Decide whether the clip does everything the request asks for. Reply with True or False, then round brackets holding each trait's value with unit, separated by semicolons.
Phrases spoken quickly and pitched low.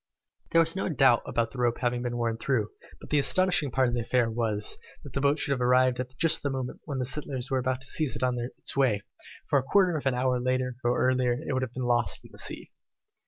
True (260 wpm; 130 Hz)